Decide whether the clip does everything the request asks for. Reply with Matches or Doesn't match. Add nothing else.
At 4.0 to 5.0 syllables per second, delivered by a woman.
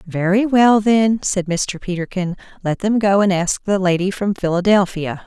Matches